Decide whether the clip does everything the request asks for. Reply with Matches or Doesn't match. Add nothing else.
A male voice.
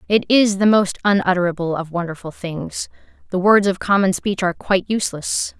Doesn't match